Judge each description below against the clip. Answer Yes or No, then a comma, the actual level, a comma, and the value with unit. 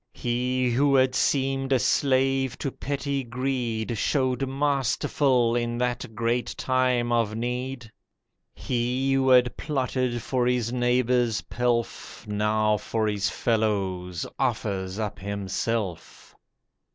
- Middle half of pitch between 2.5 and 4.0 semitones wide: Yes, average, 2.8 semitones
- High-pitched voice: No, low, 120 Hz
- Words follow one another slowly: Yes, slow, 115 wpm